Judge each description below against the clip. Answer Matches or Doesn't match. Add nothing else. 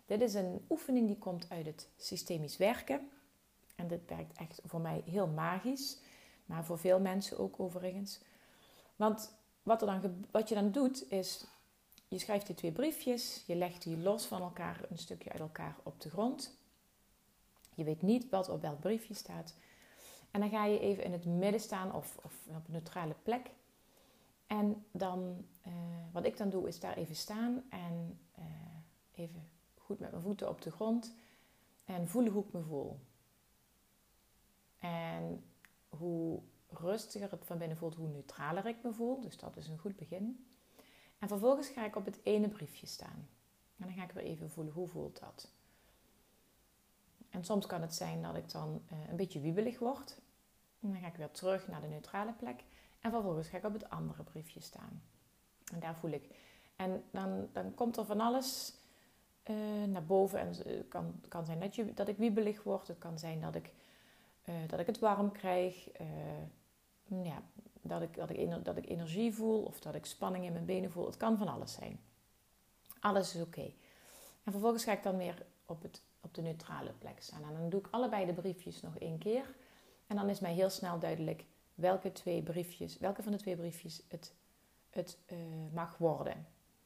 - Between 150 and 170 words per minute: Doesn't match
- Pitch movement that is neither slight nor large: Matches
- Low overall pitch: Doesn't match